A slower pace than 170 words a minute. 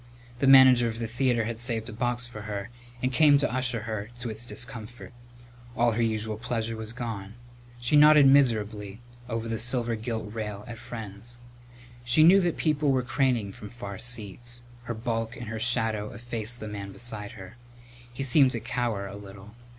No: average, 185 wpm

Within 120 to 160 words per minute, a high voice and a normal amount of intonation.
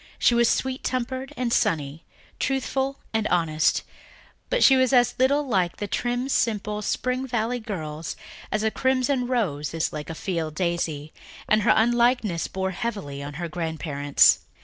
No: average, 155 wpm; high, 215 Hz; wide, 7.5 semitones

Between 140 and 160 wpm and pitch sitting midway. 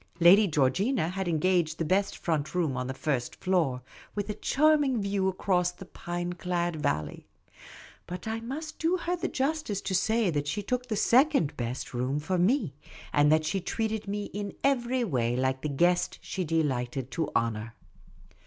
No: average, 175 wpm; medium, 180 Hz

